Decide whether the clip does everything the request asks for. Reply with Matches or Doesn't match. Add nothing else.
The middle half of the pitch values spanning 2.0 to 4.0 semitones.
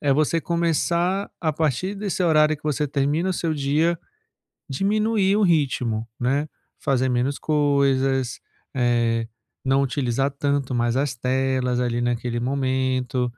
Matches